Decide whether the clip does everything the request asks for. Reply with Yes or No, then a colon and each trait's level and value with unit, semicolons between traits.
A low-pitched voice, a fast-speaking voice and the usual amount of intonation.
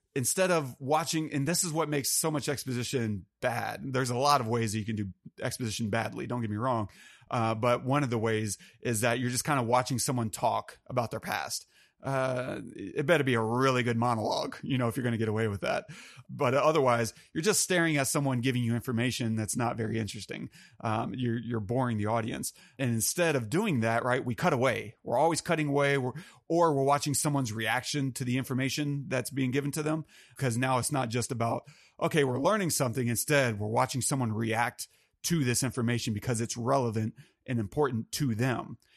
Yes: low, 125 Hz; fast, 210 wpm; average, 3.4 semitones